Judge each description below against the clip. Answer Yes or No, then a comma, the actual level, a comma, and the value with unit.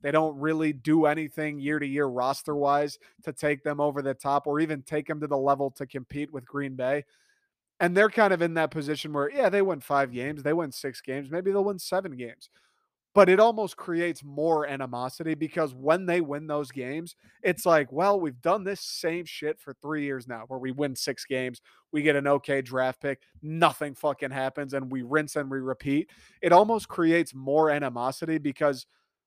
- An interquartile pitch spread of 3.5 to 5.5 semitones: No, average, 2.9 semitones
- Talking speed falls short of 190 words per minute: No, fast, 205 wpm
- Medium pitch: Yes, medium, 150 Hz